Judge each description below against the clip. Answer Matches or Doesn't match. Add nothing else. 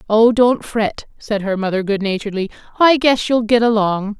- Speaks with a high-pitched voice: Matches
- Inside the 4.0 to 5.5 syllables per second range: Matches